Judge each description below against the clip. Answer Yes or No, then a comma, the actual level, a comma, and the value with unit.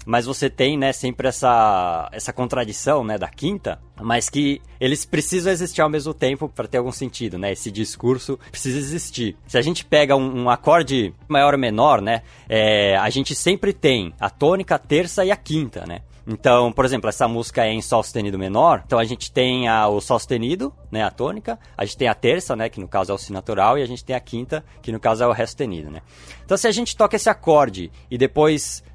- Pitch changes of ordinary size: Yes, average, 4.7 semitones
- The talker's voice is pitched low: Yes, low, 125 Hz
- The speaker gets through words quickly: Yes, fast, 225 wpm